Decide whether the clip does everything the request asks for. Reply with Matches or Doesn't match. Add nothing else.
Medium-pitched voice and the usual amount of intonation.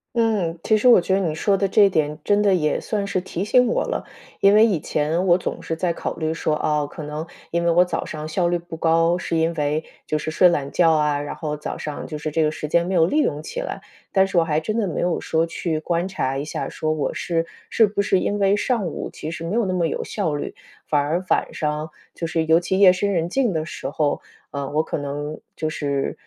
Matches